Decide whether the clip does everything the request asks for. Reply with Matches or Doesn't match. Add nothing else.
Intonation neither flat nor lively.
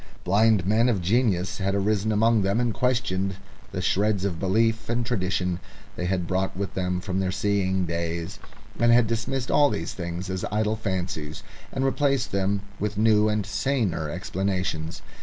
Matches